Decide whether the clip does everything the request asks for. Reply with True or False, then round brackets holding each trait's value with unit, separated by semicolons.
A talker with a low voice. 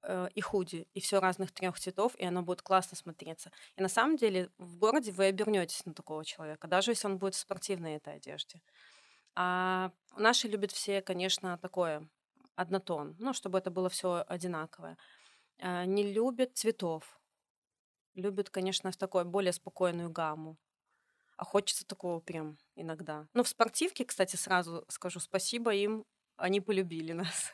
False (185 Hz)